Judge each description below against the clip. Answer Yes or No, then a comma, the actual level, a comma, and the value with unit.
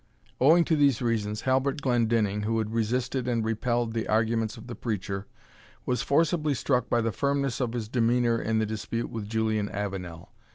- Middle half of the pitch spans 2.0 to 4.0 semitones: Yes, narrow, 2.6 semitones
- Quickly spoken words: No, average, 175 wpm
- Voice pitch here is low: Yes, low, 115 Hz